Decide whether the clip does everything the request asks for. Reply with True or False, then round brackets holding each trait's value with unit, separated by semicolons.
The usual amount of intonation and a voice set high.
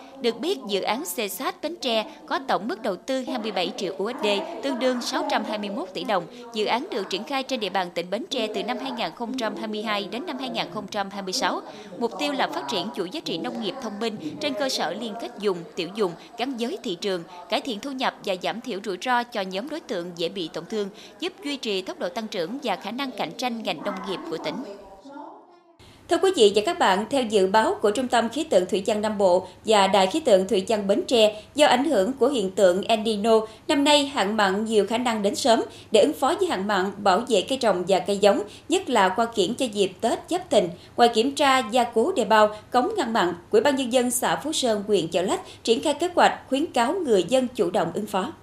True (5.0 semitones; 230 Hz)